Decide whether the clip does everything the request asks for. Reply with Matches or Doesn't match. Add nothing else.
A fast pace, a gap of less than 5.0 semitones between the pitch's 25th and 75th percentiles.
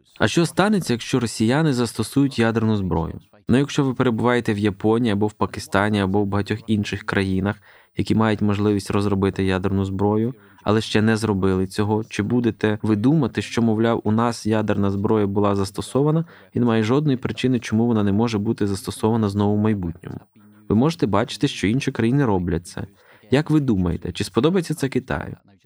Matches